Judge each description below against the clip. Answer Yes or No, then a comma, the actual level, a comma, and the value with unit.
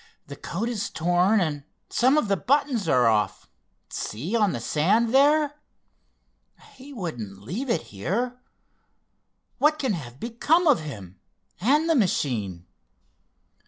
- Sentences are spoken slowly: Yes, slow, 125 wpm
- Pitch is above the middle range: Yes, high, 205 Hz